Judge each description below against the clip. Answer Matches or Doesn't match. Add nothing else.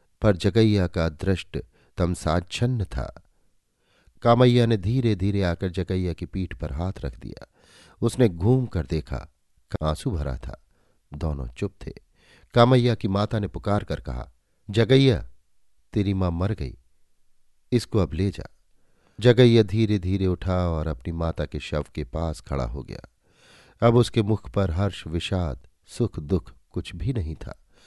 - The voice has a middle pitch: Doesn't match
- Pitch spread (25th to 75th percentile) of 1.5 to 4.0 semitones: Doesn't match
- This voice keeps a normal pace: Matches